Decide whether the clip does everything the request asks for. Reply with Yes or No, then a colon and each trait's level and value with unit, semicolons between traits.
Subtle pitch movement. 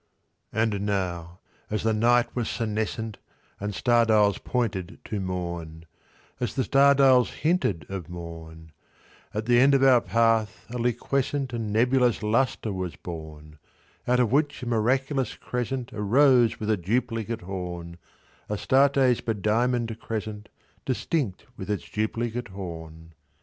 No: average, 4.6 semitones